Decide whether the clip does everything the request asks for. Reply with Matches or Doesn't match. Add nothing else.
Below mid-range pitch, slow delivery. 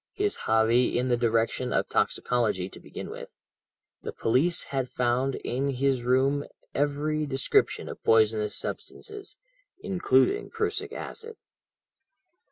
Matches